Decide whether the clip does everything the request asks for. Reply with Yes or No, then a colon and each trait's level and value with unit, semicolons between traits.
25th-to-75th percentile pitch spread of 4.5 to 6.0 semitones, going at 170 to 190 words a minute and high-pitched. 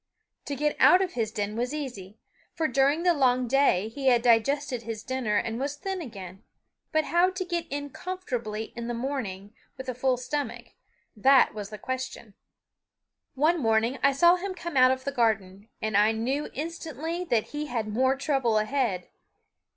Yes: average, 4.8 semitones; average, 180 wpm; very high, 260 Hz